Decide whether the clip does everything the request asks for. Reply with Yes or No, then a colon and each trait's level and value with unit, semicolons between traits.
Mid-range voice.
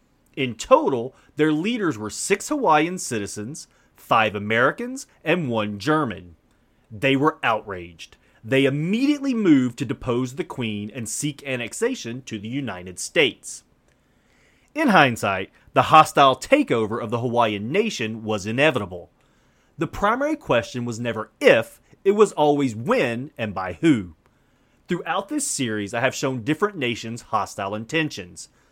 No: low, 125 Hz